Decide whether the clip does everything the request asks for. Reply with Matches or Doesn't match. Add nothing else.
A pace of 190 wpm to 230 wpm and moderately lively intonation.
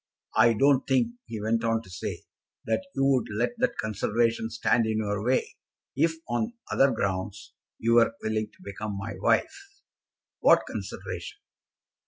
Doesn't match